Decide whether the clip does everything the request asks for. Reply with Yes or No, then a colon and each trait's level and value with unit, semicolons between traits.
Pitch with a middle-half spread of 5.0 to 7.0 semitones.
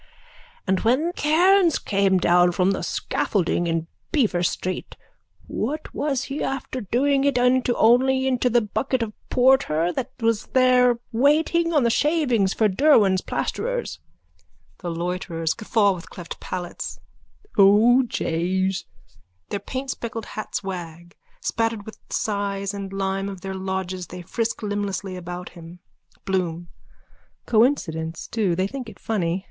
Yes: wide, 5.6 semitones